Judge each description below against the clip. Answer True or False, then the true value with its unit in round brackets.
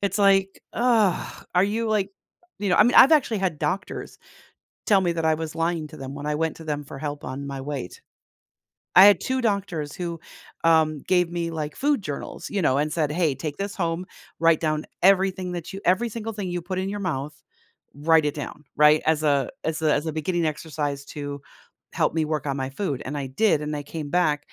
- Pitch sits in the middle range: True (160 Hz)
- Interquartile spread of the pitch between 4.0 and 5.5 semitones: True (4.3 semitones)